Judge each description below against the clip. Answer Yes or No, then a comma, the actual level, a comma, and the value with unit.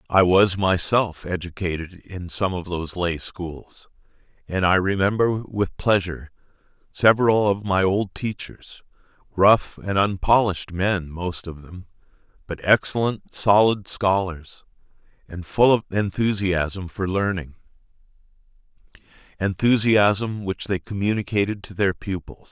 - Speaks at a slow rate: Yes, slow, 115 wpm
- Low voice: Yes, very low, 95 Hz